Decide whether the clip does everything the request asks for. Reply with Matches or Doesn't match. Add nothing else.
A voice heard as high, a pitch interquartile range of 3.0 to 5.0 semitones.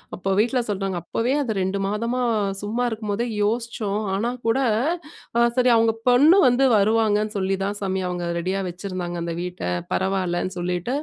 Matches